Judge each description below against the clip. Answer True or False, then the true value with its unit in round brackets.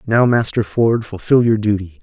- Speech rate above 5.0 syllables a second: False (4.8 syllables/s)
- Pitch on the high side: False (110 Hz)